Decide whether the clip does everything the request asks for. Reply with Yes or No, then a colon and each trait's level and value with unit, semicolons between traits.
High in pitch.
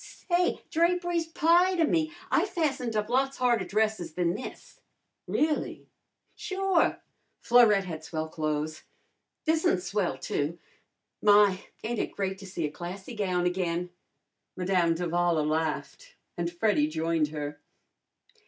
Yes: high, 195 Hz